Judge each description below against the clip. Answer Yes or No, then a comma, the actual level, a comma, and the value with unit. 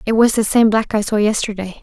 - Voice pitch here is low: No, high, 215 Hz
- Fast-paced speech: Yes, fast, 265 wpm